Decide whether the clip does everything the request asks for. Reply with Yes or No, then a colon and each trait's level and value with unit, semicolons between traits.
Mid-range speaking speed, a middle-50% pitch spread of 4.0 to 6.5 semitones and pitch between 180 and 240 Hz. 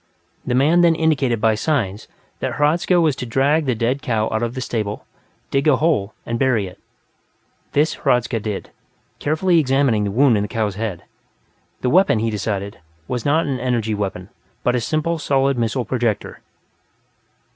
No: average, 170 wpm; average, 4.8 semitones; low, 125 Hz